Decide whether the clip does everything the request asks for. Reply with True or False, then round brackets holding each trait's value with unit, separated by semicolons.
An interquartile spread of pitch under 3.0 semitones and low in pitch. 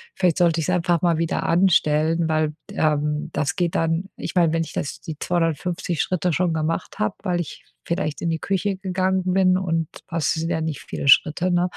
False (2.4 semitones; 165 Hz)